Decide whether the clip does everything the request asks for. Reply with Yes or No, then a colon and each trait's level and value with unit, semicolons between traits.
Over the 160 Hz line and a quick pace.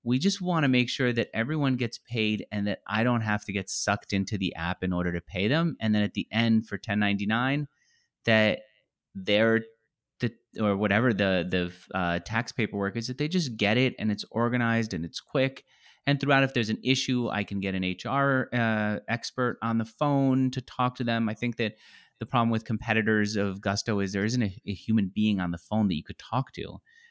No: low, 110 Hz; fast, 225 wpm